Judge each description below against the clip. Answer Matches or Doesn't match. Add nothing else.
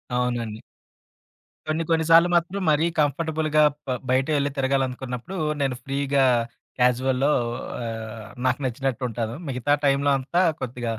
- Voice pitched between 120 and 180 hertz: Matches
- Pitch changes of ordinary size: Matches